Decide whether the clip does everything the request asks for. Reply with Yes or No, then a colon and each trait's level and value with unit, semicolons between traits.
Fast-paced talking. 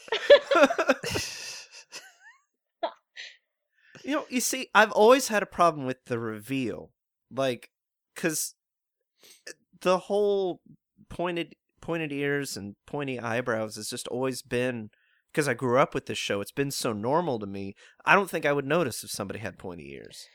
No: average, 145 wpm